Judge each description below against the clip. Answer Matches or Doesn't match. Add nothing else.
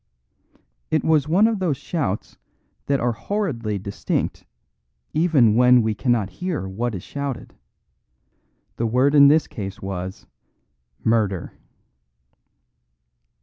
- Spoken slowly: Matches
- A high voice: Doesn't match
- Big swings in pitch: Matches